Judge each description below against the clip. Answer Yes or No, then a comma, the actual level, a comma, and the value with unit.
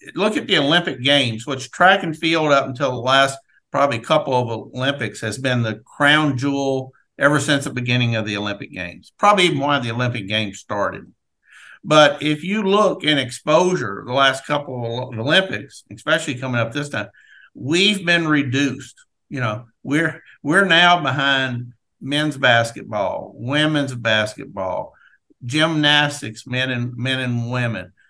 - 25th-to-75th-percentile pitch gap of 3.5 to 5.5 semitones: Yes, average, 3.8 semitones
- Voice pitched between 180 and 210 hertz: No, low, 135 Hz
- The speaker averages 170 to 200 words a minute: No, average, 155 wpm